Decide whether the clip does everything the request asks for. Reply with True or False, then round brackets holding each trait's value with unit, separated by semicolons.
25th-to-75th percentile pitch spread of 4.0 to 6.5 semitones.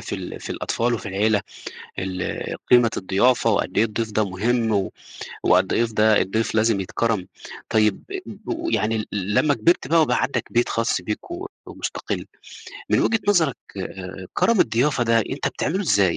False (3.6 semitones)